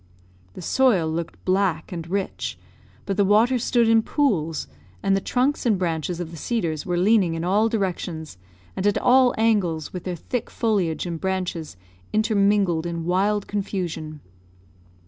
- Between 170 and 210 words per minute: No, average, 155 wpm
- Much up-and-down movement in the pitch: No, average, 4.3 semitones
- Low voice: No, high, 190 Hz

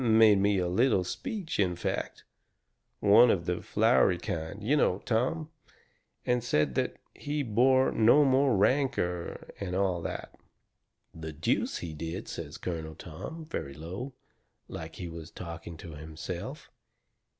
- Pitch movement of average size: No, wide, 6.8 semitones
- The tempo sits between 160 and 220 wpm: No, average, 145 wpm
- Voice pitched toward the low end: Yes, very low, 95 Hz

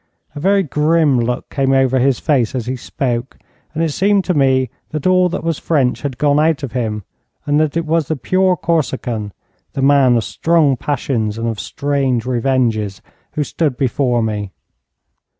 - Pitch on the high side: No, low, 135 Hz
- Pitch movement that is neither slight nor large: Yes, average, 4.2 semitones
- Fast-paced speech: No, average, 180 wpm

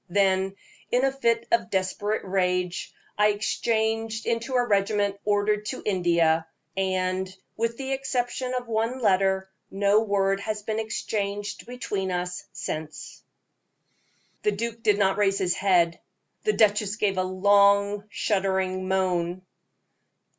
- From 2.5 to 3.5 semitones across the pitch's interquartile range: Yes, average, 2.8 semitones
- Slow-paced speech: Yes, slow, 130 wpm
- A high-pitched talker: Yes, high, 200 Hz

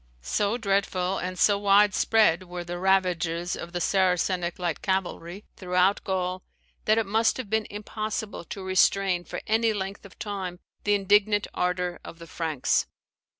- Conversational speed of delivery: Yes, average, 155 wpm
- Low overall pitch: No, high, 190 Hz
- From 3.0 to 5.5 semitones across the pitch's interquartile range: No, narrow, 2.4 semitones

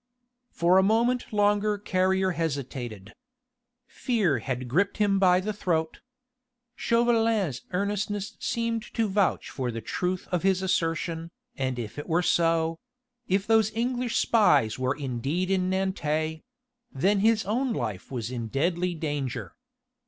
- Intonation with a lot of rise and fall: Yes, wide, 6.0 semitones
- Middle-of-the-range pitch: Yes, medium, 180 Hz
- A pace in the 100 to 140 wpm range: Yes, slow, 135 wpm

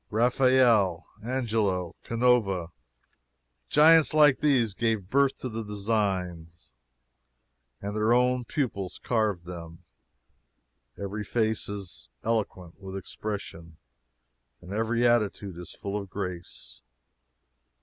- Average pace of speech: No, slow, 100 wpm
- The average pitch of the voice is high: No, low, 105 Hz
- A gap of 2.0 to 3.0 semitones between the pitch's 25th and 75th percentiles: No, average, 4.4 semitones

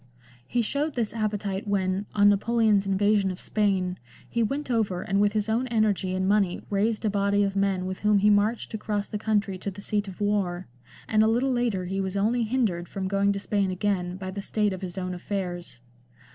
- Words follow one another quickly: Yes, fast, 210 wpm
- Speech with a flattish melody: Yes, narrow, 2.2 semitones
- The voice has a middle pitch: No, high, 200 Hz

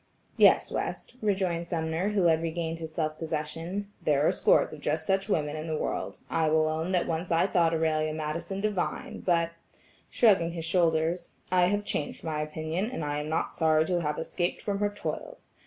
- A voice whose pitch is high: No, medium, 165 Hz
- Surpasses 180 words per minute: Yes, average, 190 wpm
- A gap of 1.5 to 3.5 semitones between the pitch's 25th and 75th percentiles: Yes, narrow, 2.5 semitones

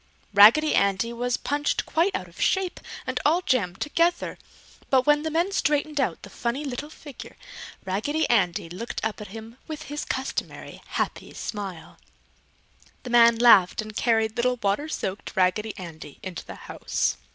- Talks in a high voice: Yes, high, 240 Hz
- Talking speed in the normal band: Yes, average, 160 wpm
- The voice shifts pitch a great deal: Yes, wide, 6.4 semitones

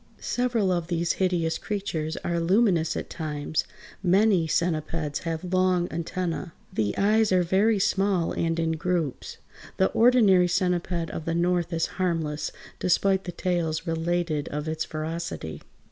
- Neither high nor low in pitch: Yes, medium, 175 Hz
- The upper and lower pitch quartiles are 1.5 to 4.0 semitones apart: Yes, narrow, 2.4 semitones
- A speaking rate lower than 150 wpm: Yes, average, 140 wpm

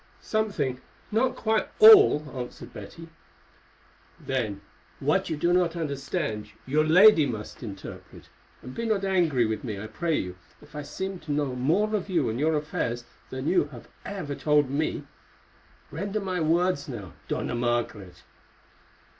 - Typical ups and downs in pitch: No, wide, 6.7 semitones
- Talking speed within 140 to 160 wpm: Yes, average, 150 wpm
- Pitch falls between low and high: Yes, medium, 150 Hz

